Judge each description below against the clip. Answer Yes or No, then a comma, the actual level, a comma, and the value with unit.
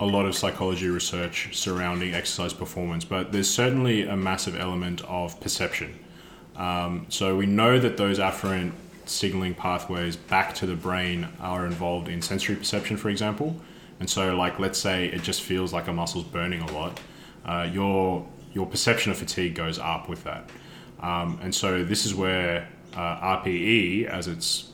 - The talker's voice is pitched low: Yes, very low, 90 Hz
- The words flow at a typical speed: Yes, average, 170 wpm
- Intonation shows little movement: Yes, narrow, 2.0 semitones